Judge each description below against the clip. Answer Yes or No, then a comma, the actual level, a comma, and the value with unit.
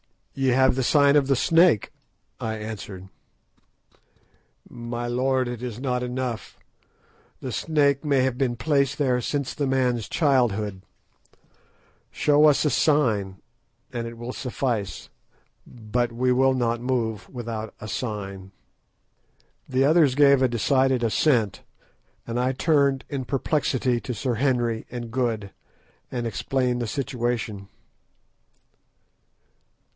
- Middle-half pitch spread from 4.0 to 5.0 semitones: No, average, 2.7 semitones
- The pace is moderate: No, slow, 125 wpm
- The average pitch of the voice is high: No, low, 125 Hz